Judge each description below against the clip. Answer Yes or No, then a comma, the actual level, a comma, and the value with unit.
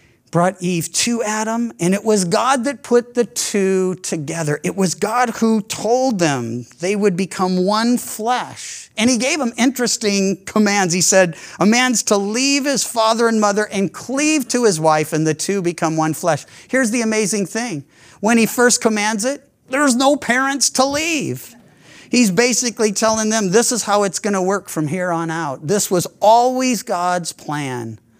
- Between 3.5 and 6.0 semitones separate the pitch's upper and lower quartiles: Yes, average, 5.1 semitones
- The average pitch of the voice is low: No, high, 210 Hz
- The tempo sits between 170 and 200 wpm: Yes, average, 180 wpm